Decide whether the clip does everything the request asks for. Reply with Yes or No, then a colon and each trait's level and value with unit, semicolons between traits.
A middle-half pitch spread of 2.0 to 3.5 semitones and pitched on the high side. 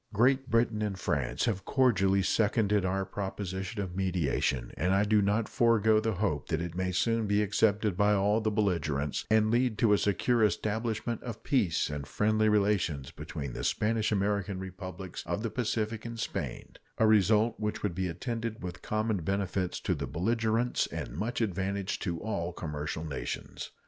No: average, 3.1 semitones; low, 100 Hz